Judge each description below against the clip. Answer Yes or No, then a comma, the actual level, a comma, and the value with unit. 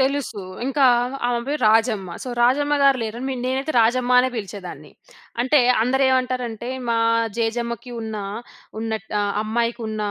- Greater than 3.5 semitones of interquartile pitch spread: No, average, 2.8 semitones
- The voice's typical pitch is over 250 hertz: No, high, 240 Hz